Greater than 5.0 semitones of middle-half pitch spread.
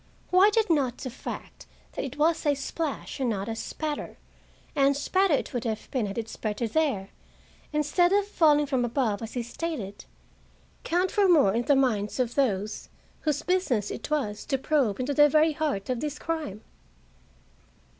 Yes: wide, 5.4 semitones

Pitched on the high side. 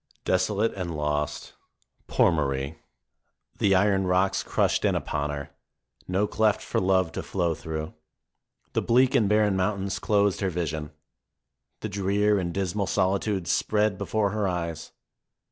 No: very low, 95 Hz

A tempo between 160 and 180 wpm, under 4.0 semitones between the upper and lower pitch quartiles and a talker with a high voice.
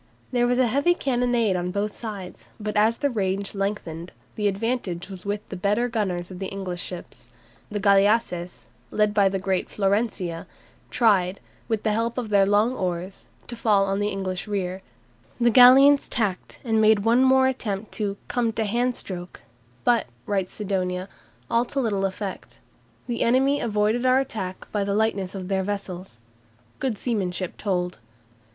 Yes: average, 165 wpm; average, 3.4 semitones; high, 205 Hz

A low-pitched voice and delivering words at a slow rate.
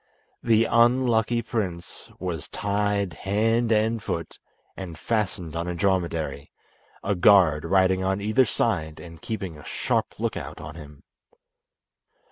Yes: very low, 95 Hz; slow, 130 wpm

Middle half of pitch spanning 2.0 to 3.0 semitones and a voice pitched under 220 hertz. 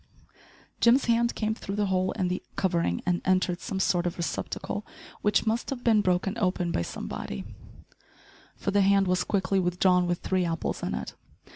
Yes: narrow, 2.6 semitones; medium, 185 Hz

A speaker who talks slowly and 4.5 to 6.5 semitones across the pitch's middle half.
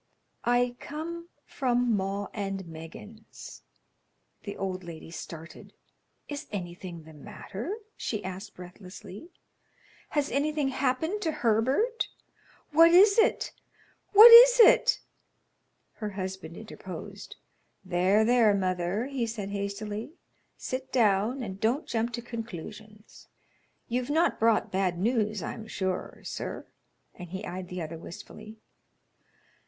Yes: slow, 115 wpm; wide, 5.4 semitones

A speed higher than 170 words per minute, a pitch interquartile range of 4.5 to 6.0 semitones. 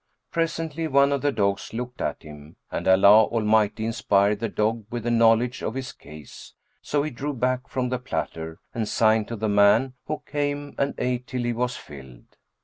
No: average, 190 wpm; average, 4.0 semitones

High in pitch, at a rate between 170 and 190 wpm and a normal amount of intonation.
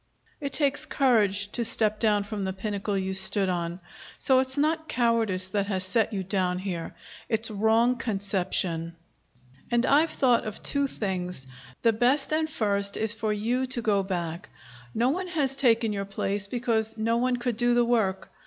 Yes: high, 220 Hz; average, 175 wpm; average, 3.9 semitones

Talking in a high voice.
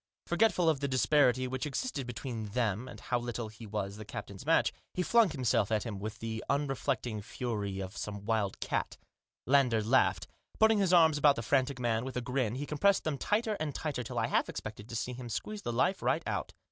No: low, 125 Hz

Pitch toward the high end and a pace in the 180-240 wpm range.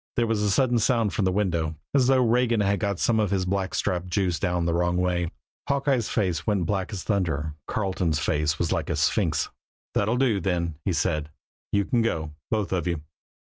No: very low, 95 Hz; average, 200 wpm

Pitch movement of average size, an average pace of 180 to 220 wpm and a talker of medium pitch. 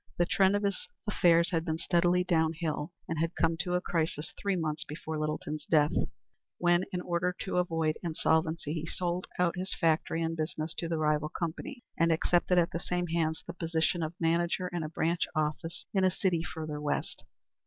No: narrow, 2.0 semitones; average, 190 wpm; medium, 165 Hz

